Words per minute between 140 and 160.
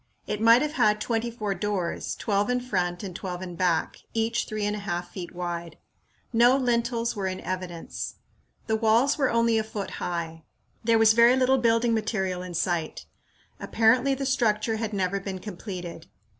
No: average, 175 wpm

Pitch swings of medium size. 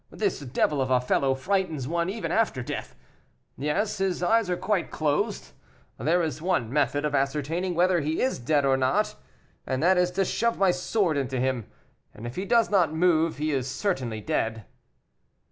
No: wide, 5.7 semitones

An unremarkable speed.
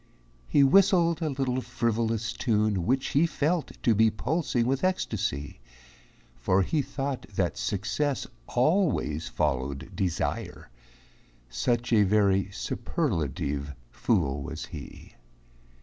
No: slow, 110 wpm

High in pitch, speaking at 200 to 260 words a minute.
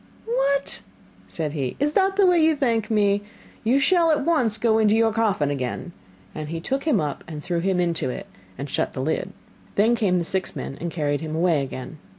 Yes: high, 205 Hz; fast, 205 wpm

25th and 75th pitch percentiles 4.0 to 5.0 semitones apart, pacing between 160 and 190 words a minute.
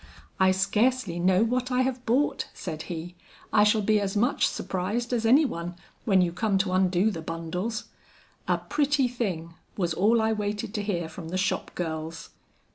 Yes: average, 4.6 semitones; average, 180 wpm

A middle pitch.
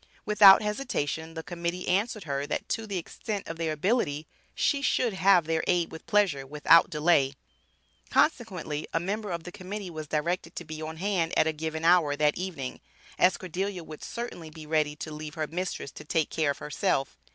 Yes: medium, 165 Hz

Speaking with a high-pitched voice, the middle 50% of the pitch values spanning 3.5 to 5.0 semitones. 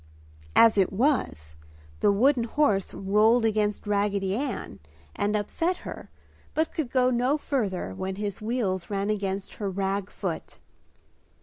Yes: high, 210 Hz; average, 3.8 semitones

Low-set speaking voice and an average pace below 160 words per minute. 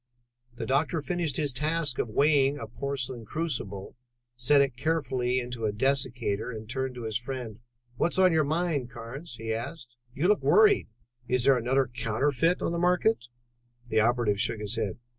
No: low, 130 Hz; average, 170 wpm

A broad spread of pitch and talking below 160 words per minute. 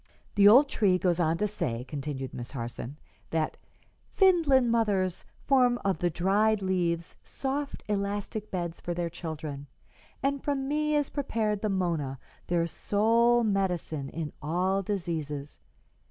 Yes: wide, 5.7 semitones; average, 140 wpm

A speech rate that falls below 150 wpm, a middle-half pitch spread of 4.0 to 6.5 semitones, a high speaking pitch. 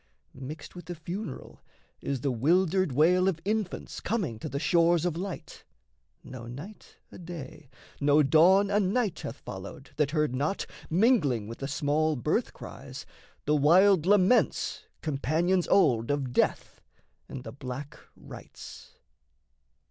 No: average, 140 wpm; average, 5.1 semitones; medium, 155 Hz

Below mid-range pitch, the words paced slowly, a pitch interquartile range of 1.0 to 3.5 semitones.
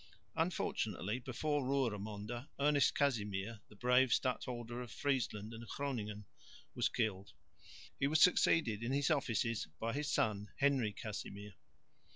No: low, 120 Hz; slow, 125 wpm; average, 4.6 semitones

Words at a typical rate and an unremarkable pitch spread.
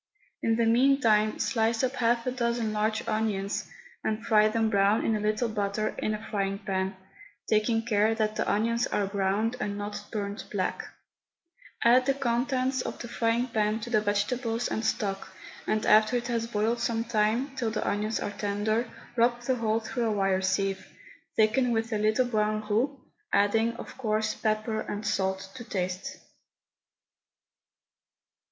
No: average, 165 wpm; narrow, 2.1 semitones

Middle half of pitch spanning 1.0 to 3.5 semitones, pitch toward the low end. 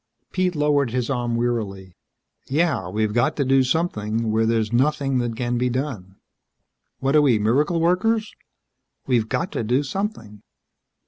No: average, 5.0 semitones; low, 125 Hz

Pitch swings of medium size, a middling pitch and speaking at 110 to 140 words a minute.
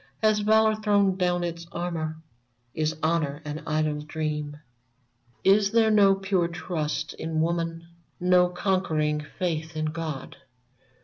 Yes: average, 3.6 semitones; medium, 170 Hz; slow, 135 wpm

